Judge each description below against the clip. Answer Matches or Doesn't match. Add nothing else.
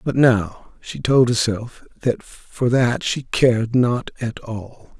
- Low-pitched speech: Matches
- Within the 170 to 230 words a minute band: Doesn't match